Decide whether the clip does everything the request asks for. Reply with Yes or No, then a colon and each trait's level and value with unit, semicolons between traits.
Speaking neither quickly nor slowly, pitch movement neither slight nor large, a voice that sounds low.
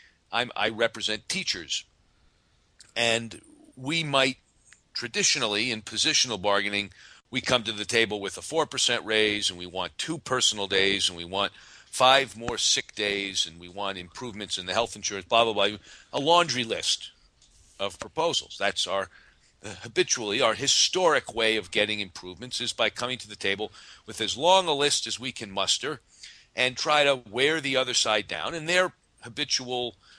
Yes: average, 170 wpm; average, 4.1 semitones; low, 110 Hz